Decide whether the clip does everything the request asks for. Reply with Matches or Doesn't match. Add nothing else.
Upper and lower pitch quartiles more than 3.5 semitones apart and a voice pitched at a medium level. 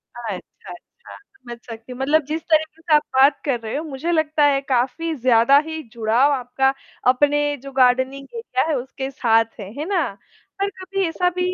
Doesn't match